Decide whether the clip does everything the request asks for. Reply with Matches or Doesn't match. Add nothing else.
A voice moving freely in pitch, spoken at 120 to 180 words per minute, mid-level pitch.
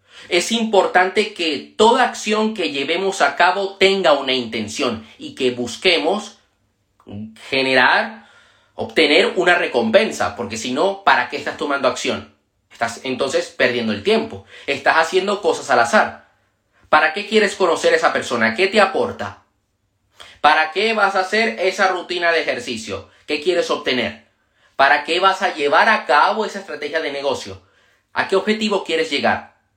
Matches